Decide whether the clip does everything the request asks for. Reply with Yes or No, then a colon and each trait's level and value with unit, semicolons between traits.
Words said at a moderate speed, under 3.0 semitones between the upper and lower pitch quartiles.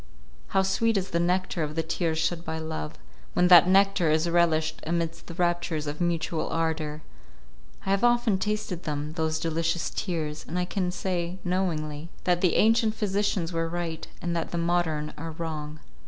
Yes: average, 175 wpm; narrow, 2.4 semitones